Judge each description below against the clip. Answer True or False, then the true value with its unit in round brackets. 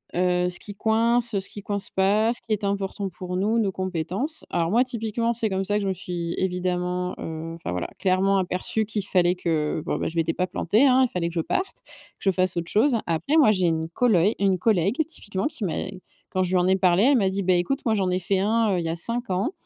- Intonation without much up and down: False (3.6 semitones)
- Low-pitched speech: False (190 Hz)